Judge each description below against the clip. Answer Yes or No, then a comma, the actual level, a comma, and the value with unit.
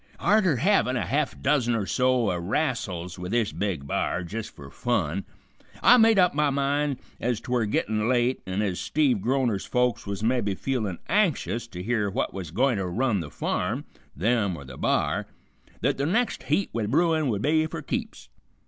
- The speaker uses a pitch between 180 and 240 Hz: No, low, 120 Hz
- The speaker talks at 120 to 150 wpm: No, average, 180 wpm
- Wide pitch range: Yes, wide, 6.2 semitones